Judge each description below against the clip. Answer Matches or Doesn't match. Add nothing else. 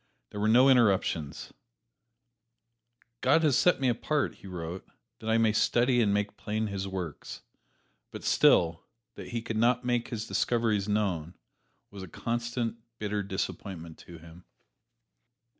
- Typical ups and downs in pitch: Matches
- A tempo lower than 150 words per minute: Matches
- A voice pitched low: Matches